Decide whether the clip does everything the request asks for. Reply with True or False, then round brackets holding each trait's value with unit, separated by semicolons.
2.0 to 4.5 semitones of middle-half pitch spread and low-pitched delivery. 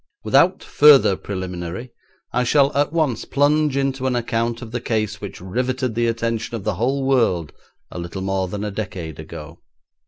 False (5.3 semitones; 115 Hz)